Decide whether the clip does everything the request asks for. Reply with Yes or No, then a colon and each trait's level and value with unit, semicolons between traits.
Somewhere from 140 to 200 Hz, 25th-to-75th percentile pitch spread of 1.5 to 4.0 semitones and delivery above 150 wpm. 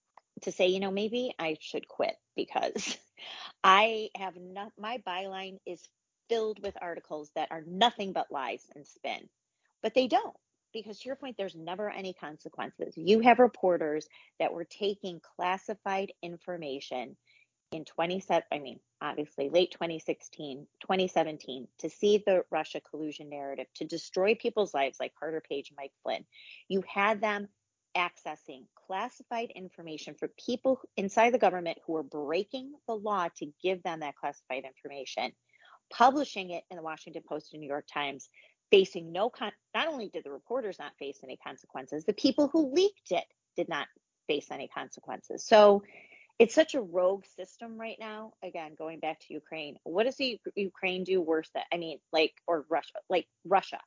No: medium, 185 Hz; average, 5.3 semitones; average, 165 wpm